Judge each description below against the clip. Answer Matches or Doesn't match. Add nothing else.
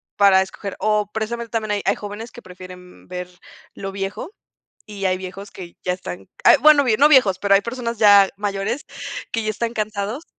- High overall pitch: Matches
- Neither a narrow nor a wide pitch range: Matches